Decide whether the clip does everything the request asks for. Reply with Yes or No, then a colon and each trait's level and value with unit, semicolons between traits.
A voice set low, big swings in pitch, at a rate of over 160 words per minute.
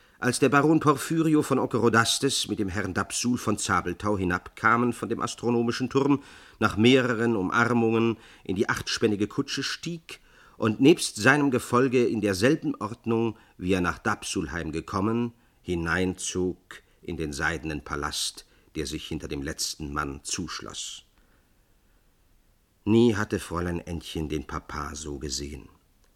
No: low, 105 Hz; wide, 5.9 semitones; average, 130 wpm